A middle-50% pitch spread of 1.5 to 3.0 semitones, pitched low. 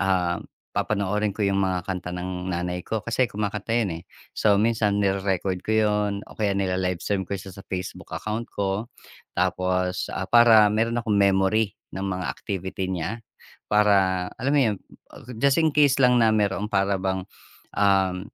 Yes: narrow, 2.5 semitones; low, 100 Hz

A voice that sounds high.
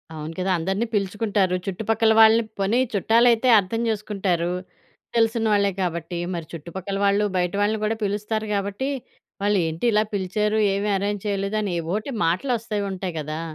Yes: high, 200 Hz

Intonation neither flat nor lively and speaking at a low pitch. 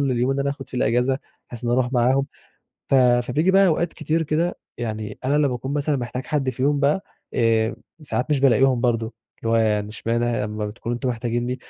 Yes: average, 3.0 semitones; low, 125 Hz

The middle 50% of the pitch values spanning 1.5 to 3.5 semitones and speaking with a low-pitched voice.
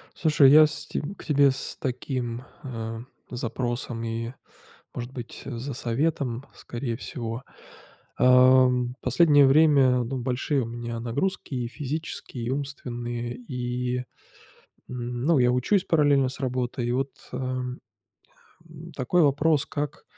Yes: average, 2.8 semitones; low, 125 Hz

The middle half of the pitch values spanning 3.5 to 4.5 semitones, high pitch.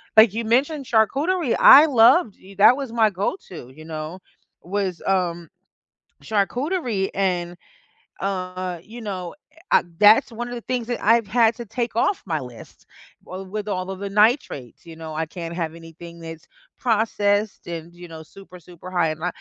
No: average, 5.0 semitones; high, 195 Hz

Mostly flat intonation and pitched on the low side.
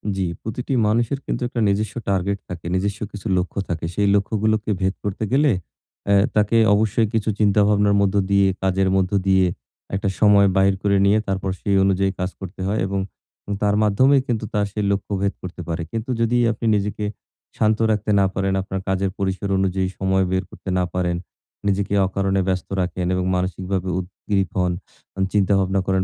Yes: narrow, 1.7 semitones; low, 100 Hz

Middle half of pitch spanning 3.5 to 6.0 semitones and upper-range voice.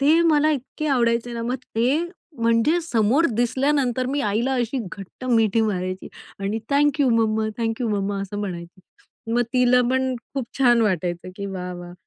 Yes: average, 4.2 semitones; high, 235 Hz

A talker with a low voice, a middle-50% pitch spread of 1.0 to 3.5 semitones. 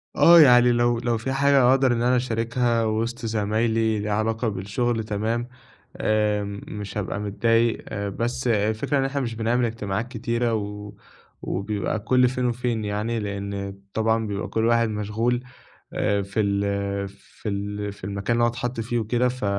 Yes: low, 110 Hz; average, 2.7 semitones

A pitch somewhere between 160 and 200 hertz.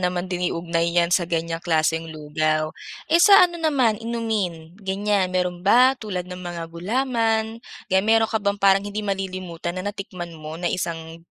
Yes: medium, 185 Hz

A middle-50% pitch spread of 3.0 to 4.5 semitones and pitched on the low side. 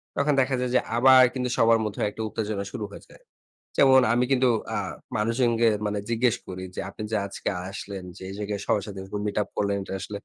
Yes: average, 3.6 semitones; low, 110 Hz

